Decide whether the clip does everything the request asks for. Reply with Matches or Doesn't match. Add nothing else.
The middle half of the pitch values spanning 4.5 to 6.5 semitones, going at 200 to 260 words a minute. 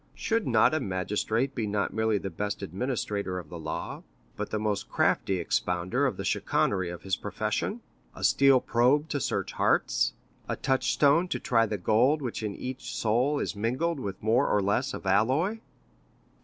Doesn't match